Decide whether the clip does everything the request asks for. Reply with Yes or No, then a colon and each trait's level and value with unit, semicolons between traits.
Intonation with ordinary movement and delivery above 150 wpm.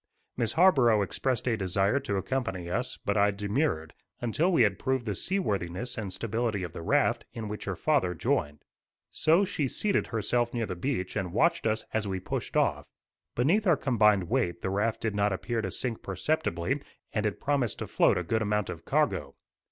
Yes: average, 4.9 semitones; average, 190 wpm